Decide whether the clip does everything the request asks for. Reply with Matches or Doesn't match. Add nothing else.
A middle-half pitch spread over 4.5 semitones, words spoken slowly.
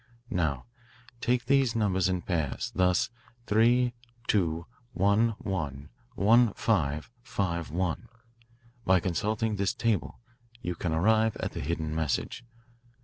Matches